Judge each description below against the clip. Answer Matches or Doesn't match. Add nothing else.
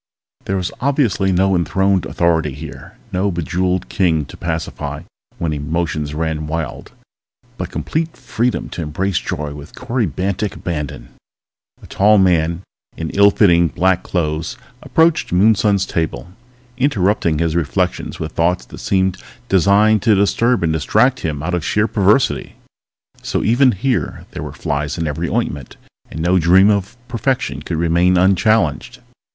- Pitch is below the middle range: Matches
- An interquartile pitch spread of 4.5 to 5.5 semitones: Doesn't match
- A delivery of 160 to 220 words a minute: Doesn't match